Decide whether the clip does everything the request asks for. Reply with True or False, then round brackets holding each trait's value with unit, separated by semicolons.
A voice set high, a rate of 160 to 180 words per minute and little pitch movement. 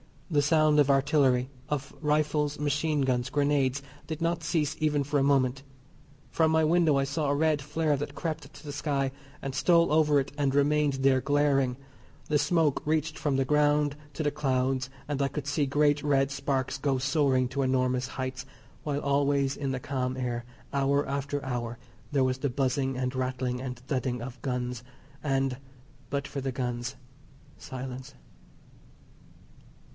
False (140 Hz; 165 wpm; 2.1 semitones)